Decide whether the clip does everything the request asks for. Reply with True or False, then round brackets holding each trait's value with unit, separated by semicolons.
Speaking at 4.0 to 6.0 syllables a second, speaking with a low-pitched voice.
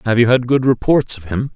True (5.6 syllables/s; 120 Hz)